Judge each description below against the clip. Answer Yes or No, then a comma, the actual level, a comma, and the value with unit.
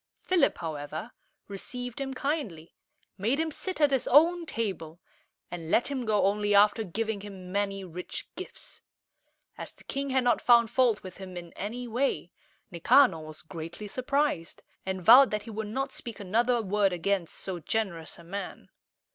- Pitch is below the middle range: No, high, 210 Hz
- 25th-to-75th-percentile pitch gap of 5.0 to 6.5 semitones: Yes, wide, 5.5 semitones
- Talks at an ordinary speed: Yes, average, 165 wpm